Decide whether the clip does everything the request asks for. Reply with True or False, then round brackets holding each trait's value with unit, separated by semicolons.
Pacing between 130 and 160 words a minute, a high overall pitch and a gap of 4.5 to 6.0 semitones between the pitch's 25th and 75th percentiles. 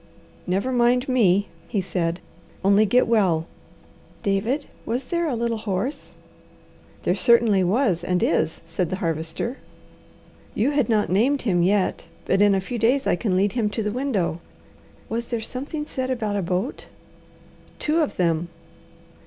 True (155 wpm; 210 Hz; 5.1 semitones)